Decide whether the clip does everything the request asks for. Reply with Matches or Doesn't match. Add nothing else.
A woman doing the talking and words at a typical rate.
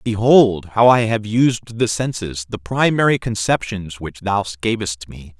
Doesn't match